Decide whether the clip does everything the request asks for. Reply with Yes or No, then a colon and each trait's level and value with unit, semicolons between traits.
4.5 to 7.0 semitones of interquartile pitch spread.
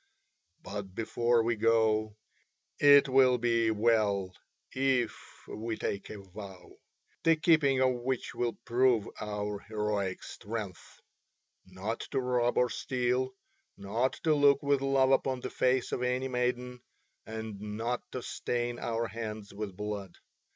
No: average, 3.3 semitones